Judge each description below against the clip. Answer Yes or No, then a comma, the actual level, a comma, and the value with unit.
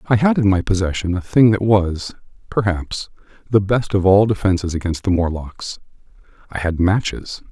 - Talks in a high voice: No, very low, 95 Hz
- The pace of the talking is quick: No, average, 160 wpm